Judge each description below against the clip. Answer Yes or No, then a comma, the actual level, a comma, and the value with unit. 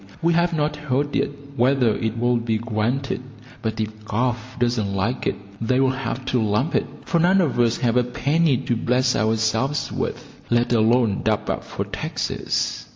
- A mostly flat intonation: No, average, 3.2 semitones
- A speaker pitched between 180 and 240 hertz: No, low, 125 Hz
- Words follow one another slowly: No, average, 175 wpm